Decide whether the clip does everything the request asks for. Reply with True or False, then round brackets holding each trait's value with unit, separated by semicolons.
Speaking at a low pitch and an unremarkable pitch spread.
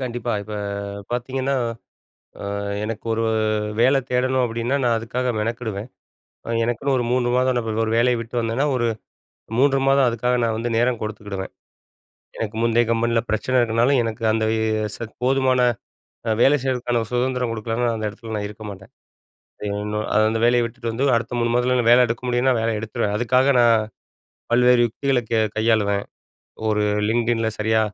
False (120 Hz; 2.0 semitones)